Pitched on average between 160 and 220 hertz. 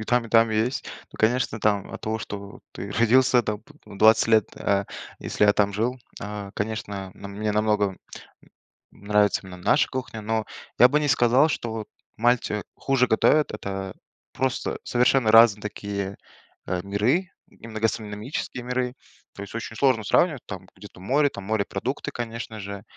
No: low, 110 Hz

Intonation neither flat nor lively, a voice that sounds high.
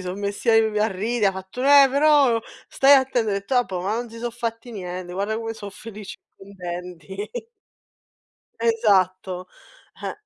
Yes: average, 3.7 semitones; high, 215 Hz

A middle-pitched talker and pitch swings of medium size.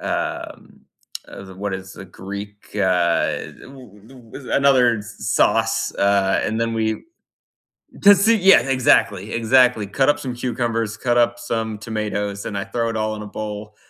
No: low, 110 Hz; average, 3.2 semitones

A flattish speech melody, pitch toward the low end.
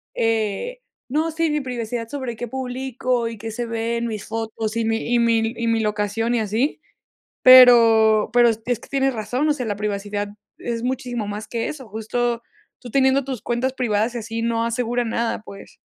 No: narrow, 2.1 semitones; high, 230 Hz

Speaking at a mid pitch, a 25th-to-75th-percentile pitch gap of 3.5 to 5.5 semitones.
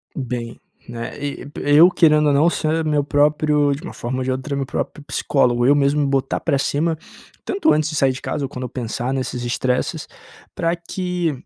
No: medium, 145 Hz; average, 3.0 semitones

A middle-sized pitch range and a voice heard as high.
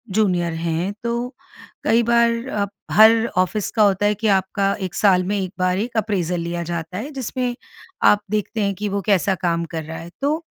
Yes: average, 3.8 semitones; high, 200 Hz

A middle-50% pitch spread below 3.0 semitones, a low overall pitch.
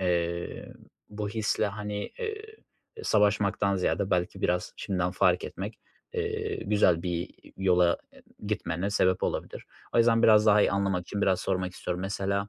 Yes: narrow, 2.6 semitones; low, 100 Hz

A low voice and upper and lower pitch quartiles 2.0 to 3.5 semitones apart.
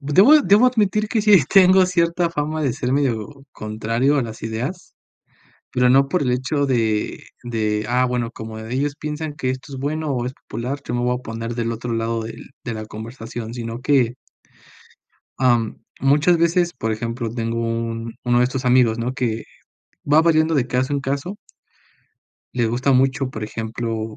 No: low, 125 Hz; average, 4.3 semitones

